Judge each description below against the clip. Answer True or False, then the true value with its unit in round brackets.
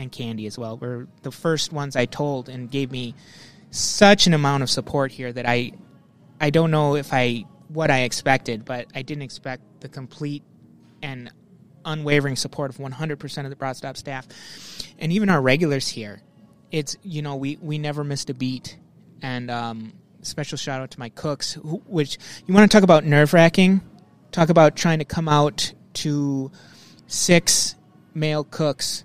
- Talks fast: False (175 wpm)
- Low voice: False (145 Hz)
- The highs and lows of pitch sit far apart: False (3.3 semitones)